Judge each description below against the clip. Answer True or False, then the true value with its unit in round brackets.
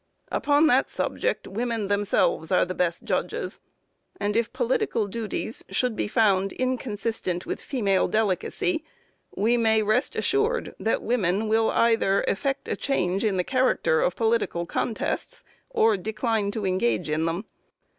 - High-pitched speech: True (220 Hz)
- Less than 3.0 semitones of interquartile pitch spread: False (4.1 semitones)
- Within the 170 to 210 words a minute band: False (145 wpm)